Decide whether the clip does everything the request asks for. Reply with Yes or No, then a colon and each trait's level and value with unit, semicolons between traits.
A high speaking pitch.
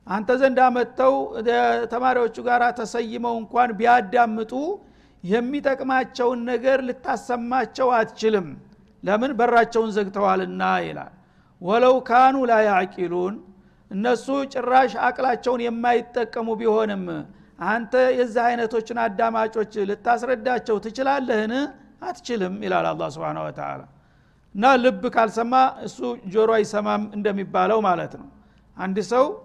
Yes: high, 235 Hz